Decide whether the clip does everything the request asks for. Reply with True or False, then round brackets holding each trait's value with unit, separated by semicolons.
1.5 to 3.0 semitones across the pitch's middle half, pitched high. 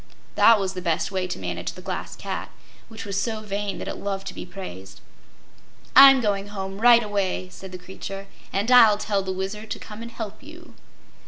True (2.5 semitones; 200 Hz)